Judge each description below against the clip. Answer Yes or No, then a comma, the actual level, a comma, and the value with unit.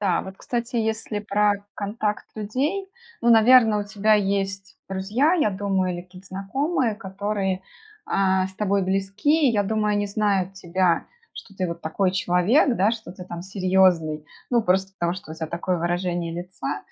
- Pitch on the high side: Yes, high, 195 Hz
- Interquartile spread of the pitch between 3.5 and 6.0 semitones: No, average, 2.7 semitones